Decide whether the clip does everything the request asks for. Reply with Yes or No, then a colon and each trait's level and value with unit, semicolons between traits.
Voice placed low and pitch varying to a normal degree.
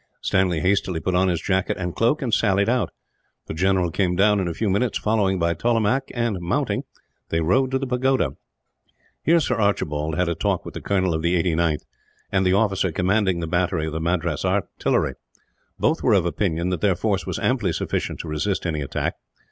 Yes: very low, 95 Hz; average, 3.9 semitones